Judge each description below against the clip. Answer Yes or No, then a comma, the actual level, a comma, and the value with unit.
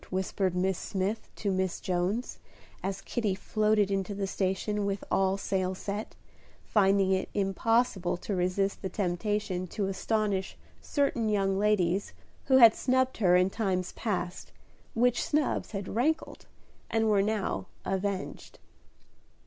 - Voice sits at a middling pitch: No, high, 195 Hz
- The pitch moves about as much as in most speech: No, narrow, 2.3 semitones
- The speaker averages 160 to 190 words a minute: No, slow, 135 wpm